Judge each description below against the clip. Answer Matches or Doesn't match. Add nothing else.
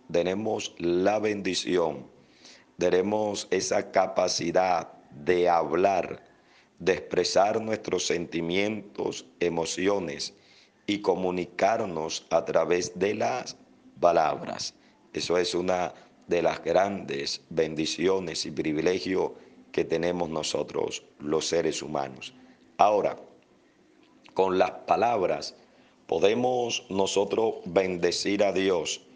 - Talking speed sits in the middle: Doesn't match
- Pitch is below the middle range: Matches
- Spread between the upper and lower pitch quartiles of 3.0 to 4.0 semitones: Matches